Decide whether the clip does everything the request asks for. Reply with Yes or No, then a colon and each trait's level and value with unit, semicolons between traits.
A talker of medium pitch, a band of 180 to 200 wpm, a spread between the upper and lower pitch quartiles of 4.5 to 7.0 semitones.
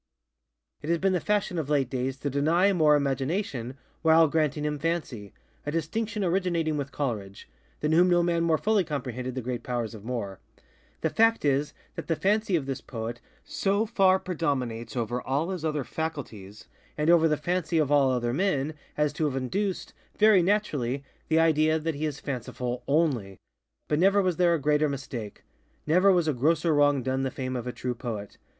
Yes: medium, 150 Hz; average, 185 wpm; average, 4.8 semitones